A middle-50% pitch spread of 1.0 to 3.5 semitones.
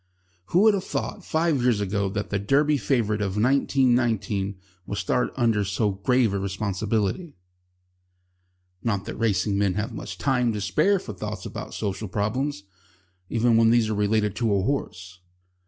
No: average, 4.0 semitones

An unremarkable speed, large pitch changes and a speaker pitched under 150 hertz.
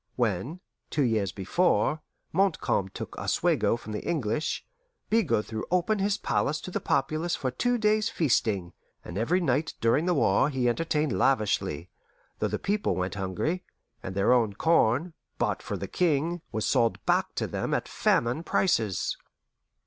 Yes: average, 155 wpm; wide, 8.3 semitones; low, 135 Hz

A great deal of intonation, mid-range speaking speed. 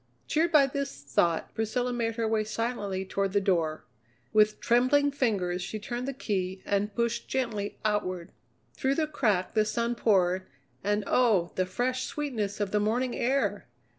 No: average, 4.2 semitones; average, 165 wpm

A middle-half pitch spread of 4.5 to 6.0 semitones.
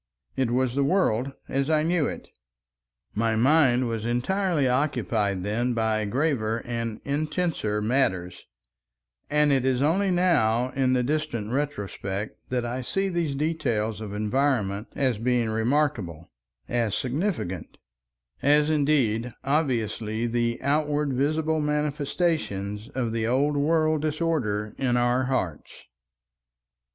Yes: average, 5.1 semitones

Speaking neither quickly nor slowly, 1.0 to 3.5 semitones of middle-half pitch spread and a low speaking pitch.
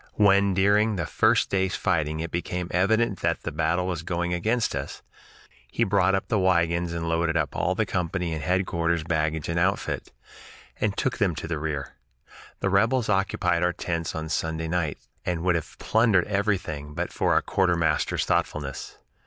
Yes: average, 175 wpm; average, 2.9 semitones; very low, 85 Hz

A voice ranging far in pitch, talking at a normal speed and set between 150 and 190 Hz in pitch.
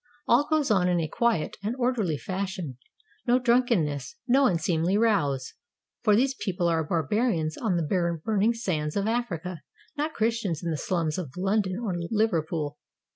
Yes: wide, 6.1 semitones; average, 160 wpm; medium, 185 Hz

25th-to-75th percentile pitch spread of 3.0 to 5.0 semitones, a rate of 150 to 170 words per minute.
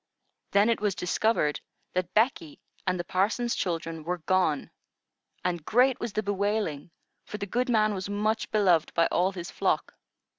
Yes: average, 3.7 semitones; average, 160 wpm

